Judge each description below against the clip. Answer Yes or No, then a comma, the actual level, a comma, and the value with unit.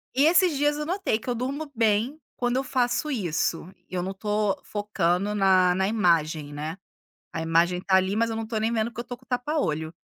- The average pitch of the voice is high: Yes, high, 215 Hz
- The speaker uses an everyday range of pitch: No, wide, 5.7 semitones